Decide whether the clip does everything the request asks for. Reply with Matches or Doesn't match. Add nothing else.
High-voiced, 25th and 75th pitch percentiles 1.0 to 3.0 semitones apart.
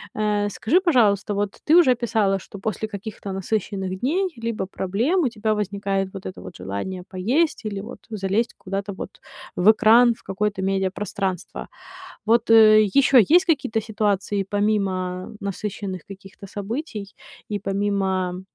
Matches